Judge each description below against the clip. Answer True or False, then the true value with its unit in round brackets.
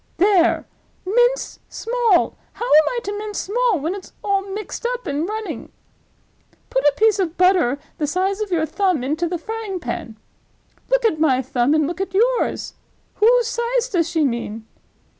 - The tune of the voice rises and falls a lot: True (6.0 semitones)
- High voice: True (380 Hz)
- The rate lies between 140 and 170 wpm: True (165 wpm)